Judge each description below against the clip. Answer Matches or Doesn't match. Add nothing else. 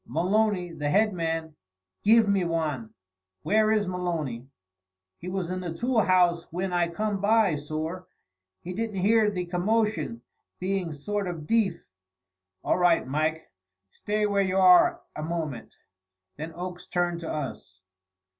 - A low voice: Doesn't match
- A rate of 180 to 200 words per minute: Doesn't match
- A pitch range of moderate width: Matches